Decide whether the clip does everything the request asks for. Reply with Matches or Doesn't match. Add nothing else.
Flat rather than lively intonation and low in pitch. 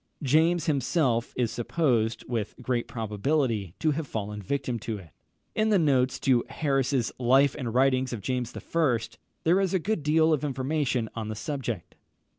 Doesn't match